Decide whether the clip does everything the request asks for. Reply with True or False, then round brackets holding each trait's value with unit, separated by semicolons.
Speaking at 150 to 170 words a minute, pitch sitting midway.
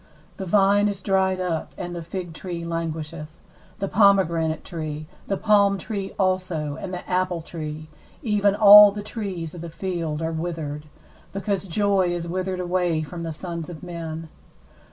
True (160 wpm; 175 Hz)